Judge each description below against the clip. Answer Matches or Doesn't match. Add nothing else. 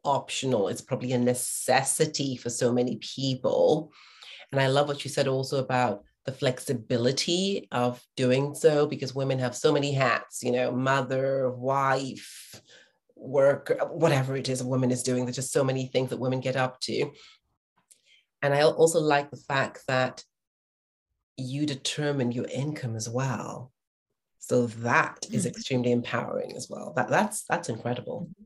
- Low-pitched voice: Matches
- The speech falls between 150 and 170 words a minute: Matches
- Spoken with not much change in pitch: Matches